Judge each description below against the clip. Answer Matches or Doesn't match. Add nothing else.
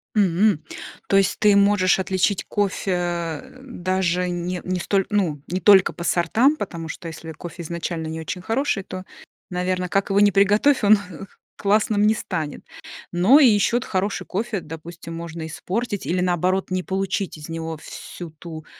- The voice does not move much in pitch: Doesn't match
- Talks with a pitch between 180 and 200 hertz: Matches